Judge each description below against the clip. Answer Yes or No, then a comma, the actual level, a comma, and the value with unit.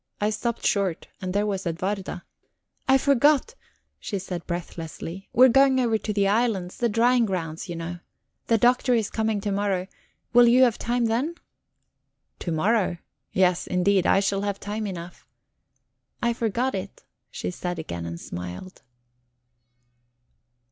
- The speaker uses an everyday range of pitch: Yes, average, 4.6 semitones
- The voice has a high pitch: Yes, high, 200 Hz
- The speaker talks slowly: No, average, 150 wpm